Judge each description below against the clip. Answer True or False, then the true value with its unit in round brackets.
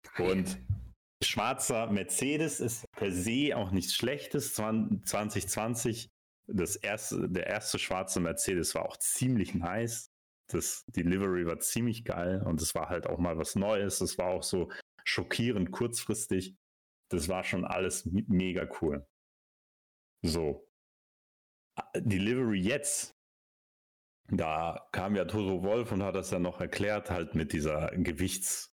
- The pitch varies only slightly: False (4.4 semitones)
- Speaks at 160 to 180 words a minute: False (130 wpm)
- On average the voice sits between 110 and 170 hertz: False (95 Hz)